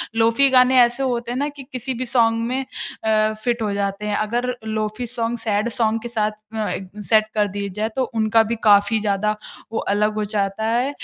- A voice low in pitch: No, high, 225 Hz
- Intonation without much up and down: Yes, narrow, 2.3 semitones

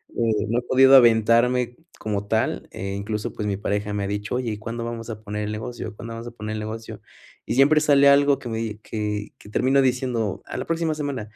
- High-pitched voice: No, low, 115 Hz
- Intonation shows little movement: No, average, 3.1 semitones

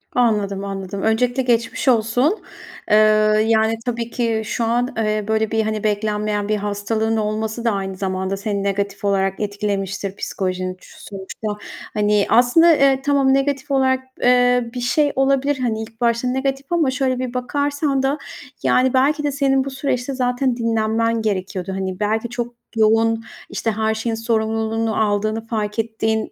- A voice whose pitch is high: Yes, high, 225 Hz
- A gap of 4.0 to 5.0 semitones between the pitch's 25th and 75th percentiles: No, average, 3.3 semitones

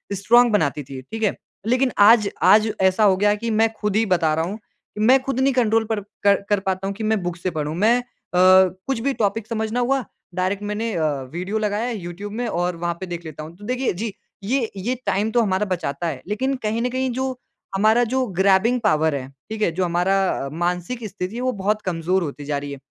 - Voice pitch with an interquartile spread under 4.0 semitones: No, average, 4.5 semitones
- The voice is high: Yes, high, 205 Hz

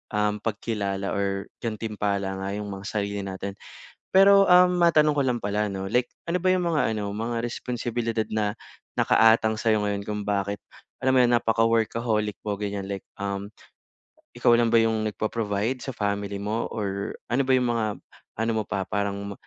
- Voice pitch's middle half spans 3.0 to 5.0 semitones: No, narrow, 2.6 semitones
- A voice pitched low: Yes, low, 105 Hz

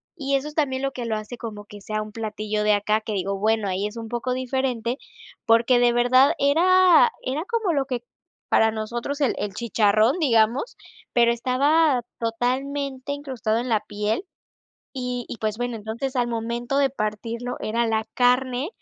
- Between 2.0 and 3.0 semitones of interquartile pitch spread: No, average, 3.6 semitones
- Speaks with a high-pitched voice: Yes, high, 240 Hz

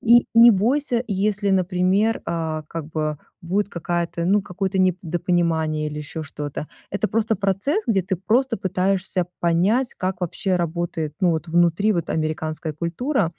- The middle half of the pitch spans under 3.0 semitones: No, average, 3.7 semitones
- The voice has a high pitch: No, medium, 180 Hz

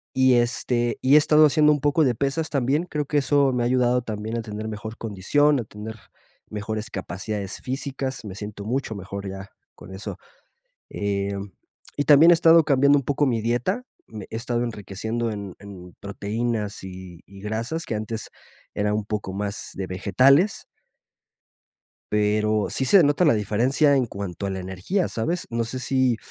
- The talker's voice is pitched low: Yes, low, 115 Hz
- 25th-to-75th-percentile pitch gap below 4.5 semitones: No, average, 5.0 semitones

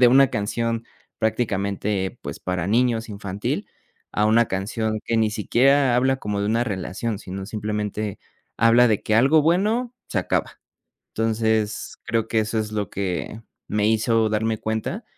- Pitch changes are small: Yes, narrow, 2.1 semitones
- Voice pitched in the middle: No, low, 110 Hz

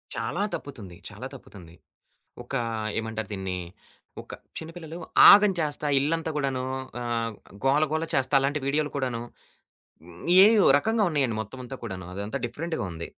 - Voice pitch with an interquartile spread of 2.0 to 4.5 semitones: No, wide, 5.6 semitones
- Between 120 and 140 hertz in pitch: Yes, low, 135 Hz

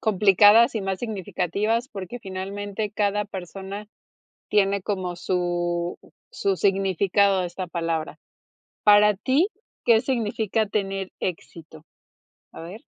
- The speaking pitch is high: Yes, high, 195 Hz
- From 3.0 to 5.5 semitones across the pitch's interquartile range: No, narrow, 2.5 semitones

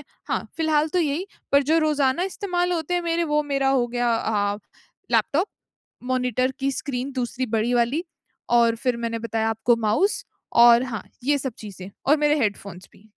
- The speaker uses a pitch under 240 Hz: No, very high, 255 Hz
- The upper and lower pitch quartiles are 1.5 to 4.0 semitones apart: No, average, 4.7 semitones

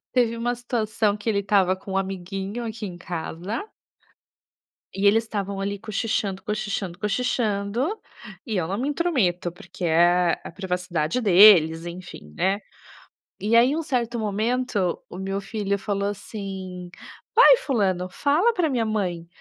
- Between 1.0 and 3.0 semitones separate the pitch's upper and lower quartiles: No, average, 3.8 semitones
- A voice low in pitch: No, high, 200 Hz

